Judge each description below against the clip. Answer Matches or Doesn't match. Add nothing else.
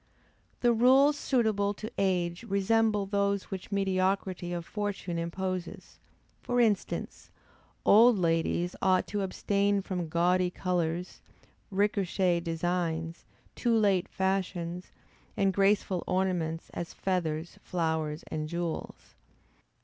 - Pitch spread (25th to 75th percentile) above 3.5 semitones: Doesn't match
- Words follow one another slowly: Matches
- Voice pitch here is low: Doesn't match